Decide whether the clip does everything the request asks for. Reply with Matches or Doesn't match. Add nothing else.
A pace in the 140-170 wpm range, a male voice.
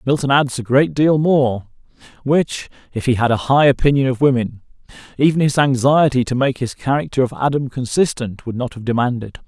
Doesn't match